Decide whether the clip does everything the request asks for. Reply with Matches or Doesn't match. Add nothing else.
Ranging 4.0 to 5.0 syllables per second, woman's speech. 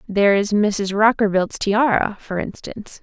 Matches